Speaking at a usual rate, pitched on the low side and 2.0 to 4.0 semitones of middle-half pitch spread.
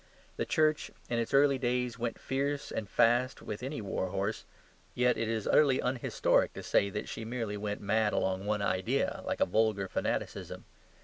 Yes: average, 175 wpm; low, 115 Hz; average, 3.7 semitones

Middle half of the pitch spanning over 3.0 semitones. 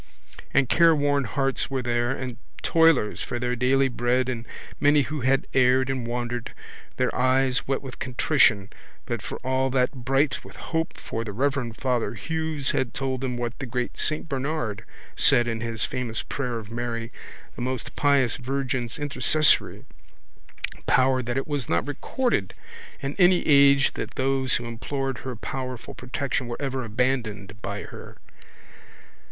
No: narrow, 2.5 semitones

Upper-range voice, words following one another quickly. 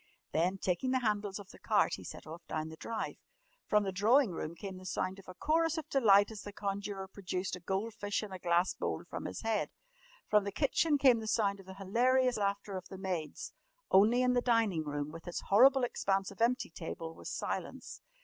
Yes: high, 200 Hz; fast, 215 wpm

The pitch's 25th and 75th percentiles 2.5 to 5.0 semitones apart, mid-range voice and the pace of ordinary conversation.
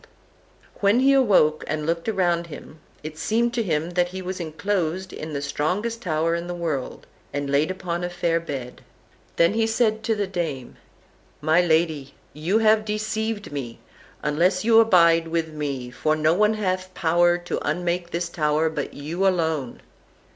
Yes: average, 3.9 semitones; medium, 170 Hz; average, 170 wpm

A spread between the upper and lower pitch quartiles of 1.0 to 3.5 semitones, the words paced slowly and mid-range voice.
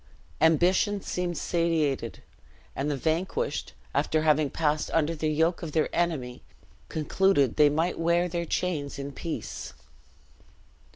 Yes: narrow, 2.6 semitones; slow, 125 wpm; medium, 160 Hz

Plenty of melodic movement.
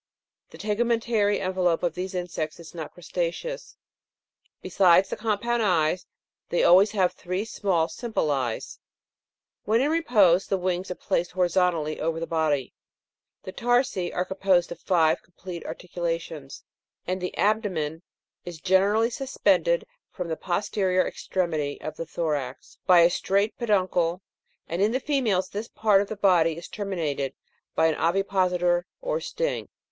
No: average, 3.5 semitones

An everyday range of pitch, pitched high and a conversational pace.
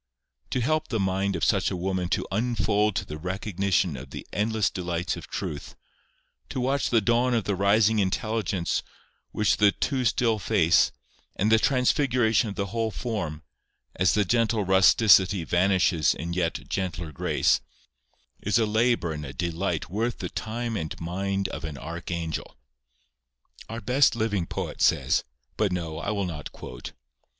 No: average, 4.6 semitones; low, 100 Hz; average, 160 wpm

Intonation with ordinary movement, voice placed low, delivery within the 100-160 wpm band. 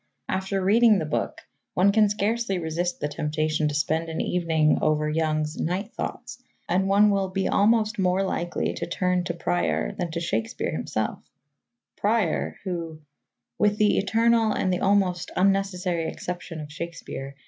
No: average, 3.9 semitones; medium, 180 Hz; average, 150 wpm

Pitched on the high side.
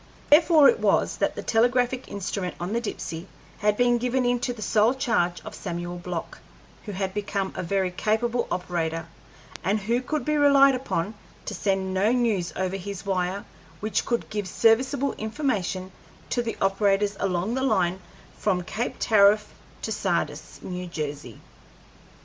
Yes: high, 205 Hz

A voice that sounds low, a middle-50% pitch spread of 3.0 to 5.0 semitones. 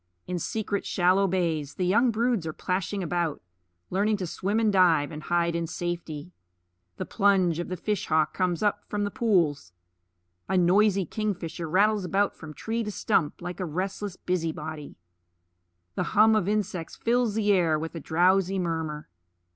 No: medium, 180 Hz; average, 3.7 semitones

